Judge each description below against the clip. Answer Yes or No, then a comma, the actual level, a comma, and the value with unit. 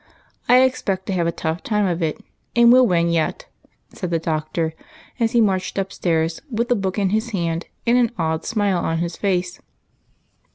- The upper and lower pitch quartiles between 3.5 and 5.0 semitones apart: Yes, average, 4.6 semitones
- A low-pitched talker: No, medium, 185 Hz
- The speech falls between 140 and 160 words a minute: No, average, 195 wpm